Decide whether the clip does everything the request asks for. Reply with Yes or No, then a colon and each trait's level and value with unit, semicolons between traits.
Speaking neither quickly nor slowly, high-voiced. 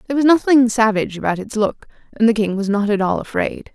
No: fast, 240 wpm; high, 225 Hz